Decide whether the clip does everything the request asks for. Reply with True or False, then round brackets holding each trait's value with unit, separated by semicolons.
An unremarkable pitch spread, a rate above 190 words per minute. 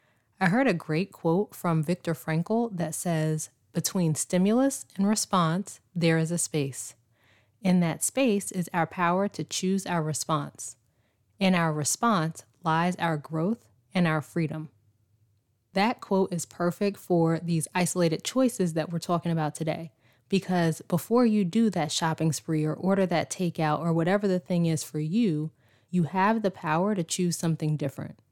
False (3.3 semitones; 160 wpm)